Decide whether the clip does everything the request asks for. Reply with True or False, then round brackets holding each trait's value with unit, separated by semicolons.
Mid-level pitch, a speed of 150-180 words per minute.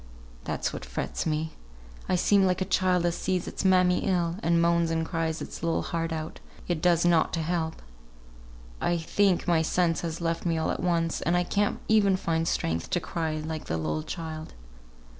False (170 Hz; 195 wpm)